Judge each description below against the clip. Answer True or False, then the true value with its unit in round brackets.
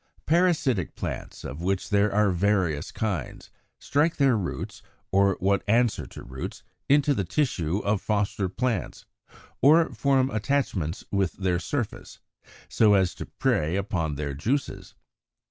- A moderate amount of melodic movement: False (6.4 semitones)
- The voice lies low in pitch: True (100 Hz)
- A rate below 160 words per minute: True (140 wpm)